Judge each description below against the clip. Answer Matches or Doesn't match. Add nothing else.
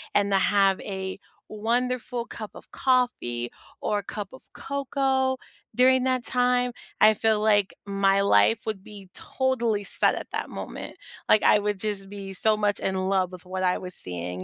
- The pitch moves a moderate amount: Matches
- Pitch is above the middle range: Matches